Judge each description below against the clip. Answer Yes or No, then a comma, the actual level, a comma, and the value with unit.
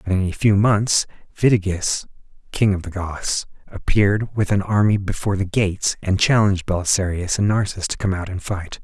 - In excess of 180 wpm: Yes, average, 190 wpm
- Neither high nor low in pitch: No, low, 100 Hz